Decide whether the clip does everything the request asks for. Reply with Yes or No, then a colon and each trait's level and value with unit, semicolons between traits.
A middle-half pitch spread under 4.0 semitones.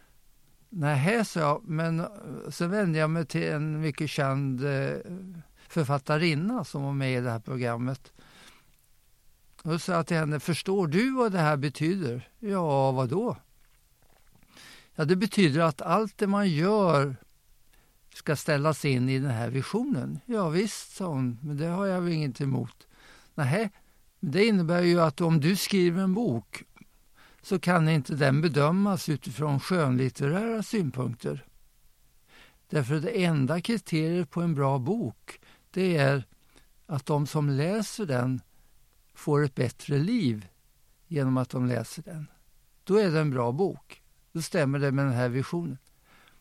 No: average, 4.8 semitones